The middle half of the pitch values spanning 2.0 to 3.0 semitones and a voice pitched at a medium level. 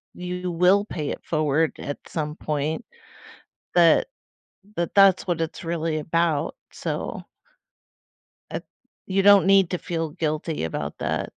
Yes: average, 2.7 semitones; medium, 165 Hz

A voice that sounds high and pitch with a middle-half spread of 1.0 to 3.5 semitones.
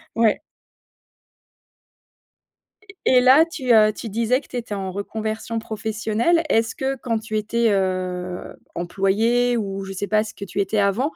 Yes: high, 220 Hz; average, 3.1 semitones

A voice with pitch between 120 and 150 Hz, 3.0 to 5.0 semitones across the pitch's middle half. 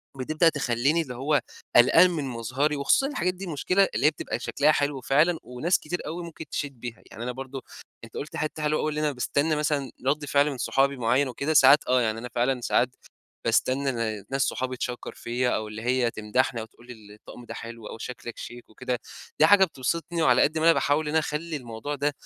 Yes: medium, 140 Hz; average, 3.8 semitones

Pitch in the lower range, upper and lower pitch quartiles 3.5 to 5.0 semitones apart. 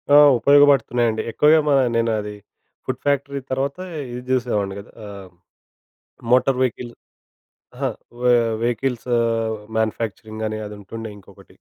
No: low, 115 Hz; average, 3.0 semitones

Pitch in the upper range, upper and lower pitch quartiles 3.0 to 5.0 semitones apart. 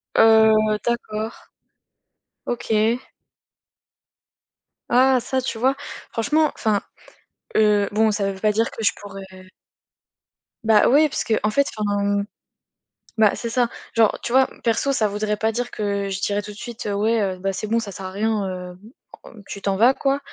No: high, 215 Hz; narrow, 2.6 semitones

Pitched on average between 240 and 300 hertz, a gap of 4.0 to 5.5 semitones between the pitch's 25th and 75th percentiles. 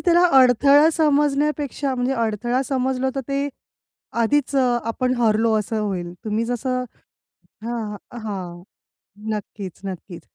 Yes: high, 245 Hz; average, 4.3 semitones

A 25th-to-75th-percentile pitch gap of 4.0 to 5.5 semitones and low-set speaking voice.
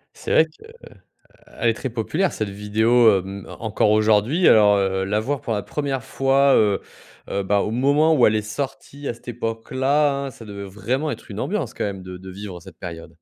Yes: average, 5.1 semitones; low, 110 Hz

